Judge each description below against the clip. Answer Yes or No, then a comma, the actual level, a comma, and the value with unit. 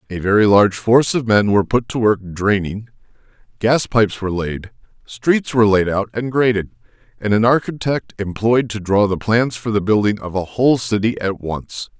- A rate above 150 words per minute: Yes, average, 190 wpm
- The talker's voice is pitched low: Yes, low, 110 Hz